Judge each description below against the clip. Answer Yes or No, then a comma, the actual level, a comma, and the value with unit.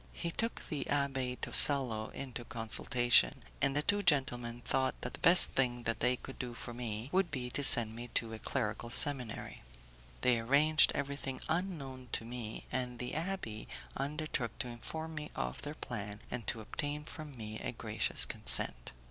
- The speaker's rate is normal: Yes, average, 170 wpm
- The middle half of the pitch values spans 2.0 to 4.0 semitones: Yes, average, 3.7 semitones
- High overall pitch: No, low, 125 Hz